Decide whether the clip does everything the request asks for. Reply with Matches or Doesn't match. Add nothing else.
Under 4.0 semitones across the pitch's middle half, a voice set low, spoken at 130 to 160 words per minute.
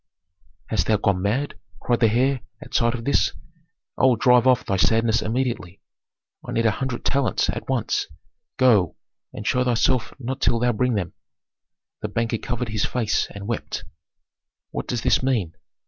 Doesn't match